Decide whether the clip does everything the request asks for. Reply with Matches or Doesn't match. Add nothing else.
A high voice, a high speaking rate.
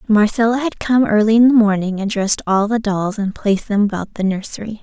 Matches